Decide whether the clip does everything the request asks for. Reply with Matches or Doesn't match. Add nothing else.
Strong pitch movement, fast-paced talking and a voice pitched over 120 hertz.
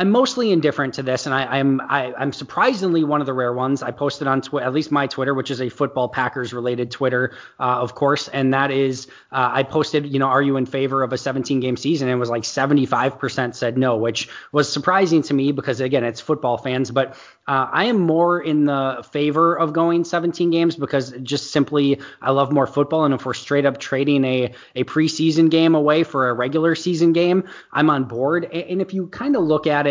Doesn't match